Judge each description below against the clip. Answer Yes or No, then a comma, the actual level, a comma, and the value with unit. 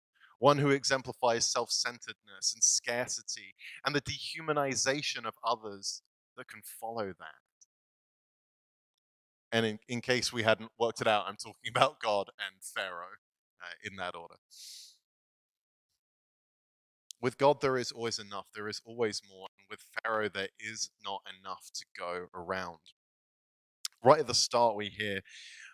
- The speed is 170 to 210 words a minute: No, average, 140 wpm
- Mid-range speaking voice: No, low, 110 Hz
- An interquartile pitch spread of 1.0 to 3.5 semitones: No, average, 4.2 semitones